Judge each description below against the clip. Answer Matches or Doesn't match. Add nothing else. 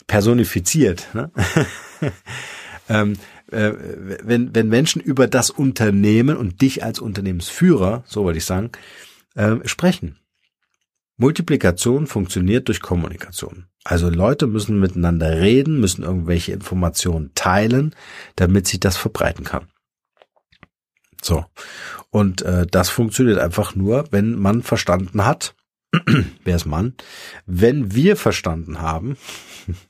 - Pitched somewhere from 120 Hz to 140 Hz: Doesn't match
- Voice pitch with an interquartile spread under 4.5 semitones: Doesn't match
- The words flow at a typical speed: Doesn't match